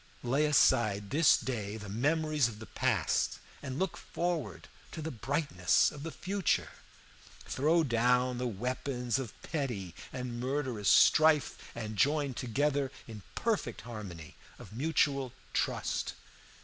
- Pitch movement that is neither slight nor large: Yes, average, 4.4 semitones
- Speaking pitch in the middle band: No, low, 130 Hz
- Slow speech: Yes, slow, 130 wpm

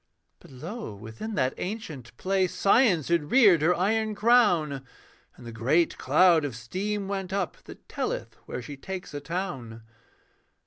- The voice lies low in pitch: No, medium, 175 Hz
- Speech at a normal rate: Yes, average, 150 wpm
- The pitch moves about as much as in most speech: No, wide, 6.6 semitones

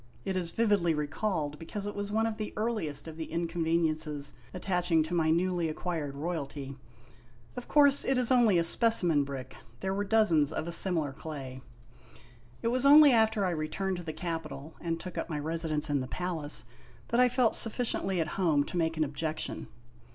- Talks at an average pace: Yes, average, 185 wpm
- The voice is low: No, medium, 170 Hz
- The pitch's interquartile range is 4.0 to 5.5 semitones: Yes, average, 4.8 semitones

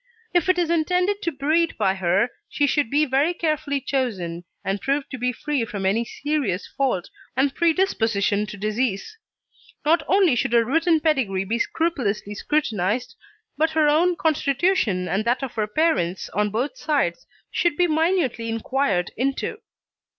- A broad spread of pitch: Yes, wide, 7.2 semitones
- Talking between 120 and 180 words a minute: Yes, average, 160 wpm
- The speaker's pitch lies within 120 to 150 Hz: No, very high, 270 Hz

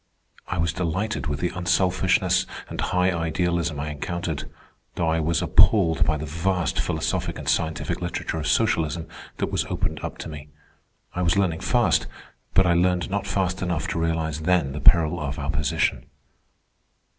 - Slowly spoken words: No, average, 170 wpm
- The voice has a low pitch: Yes, very low, 85 Hz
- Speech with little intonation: Yes, narrow, 2.3 semitones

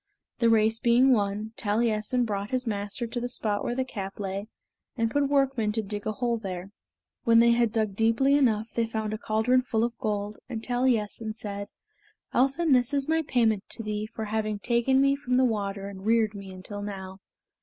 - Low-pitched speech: No, high, 225 Hz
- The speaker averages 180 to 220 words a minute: Yes, average, 200 wpm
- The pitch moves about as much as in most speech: Yes, average, 3.0 semitones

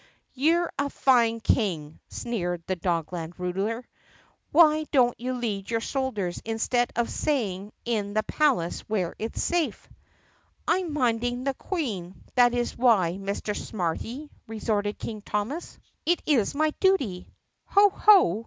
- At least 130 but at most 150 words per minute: Yes, slow, 135 wpm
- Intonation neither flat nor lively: No, wide, 5.7 semitones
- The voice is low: No, high, 230 Hz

